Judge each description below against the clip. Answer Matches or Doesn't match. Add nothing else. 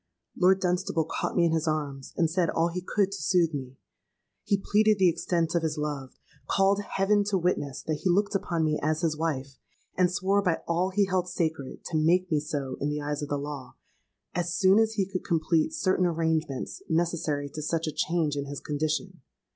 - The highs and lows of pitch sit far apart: Doesn't match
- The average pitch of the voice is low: Doesn't match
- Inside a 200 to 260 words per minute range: Matches